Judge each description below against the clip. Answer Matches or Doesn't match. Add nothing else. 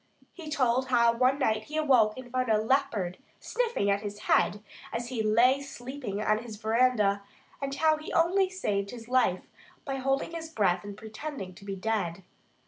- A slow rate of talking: Doesn't match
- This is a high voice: Matches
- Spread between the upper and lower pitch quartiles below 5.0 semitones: Matches